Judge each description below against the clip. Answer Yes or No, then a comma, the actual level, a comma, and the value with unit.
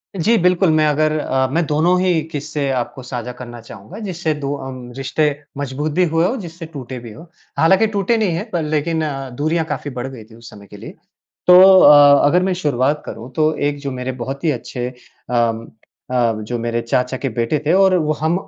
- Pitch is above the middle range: No, medium, 150 Hz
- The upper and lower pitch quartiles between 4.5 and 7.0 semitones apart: Yes, average, 4.8 semitones